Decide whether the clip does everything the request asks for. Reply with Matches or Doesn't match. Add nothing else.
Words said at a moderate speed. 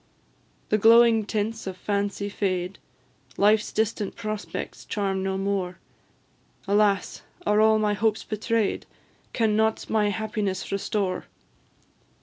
Doesn't match